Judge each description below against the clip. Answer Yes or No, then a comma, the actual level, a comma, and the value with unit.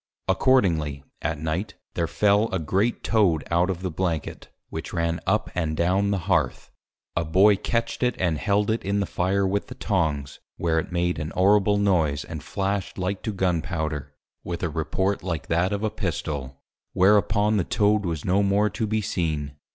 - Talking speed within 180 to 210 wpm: Yes, average, 185 wpm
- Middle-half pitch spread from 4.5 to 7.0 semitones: No, average, 4.0 semitones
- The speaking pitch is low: Yes, very low, 95 Hz